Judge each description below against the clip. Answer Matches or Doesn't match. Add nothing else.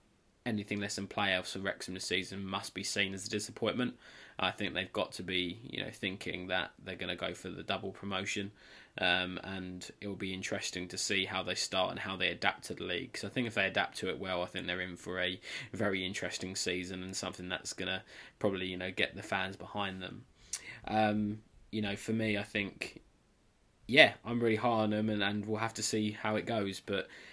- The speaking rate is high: Matches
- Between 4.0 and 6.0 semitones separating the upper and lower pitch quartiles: Doesn't match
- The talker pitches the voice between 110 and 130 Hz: Doesn't match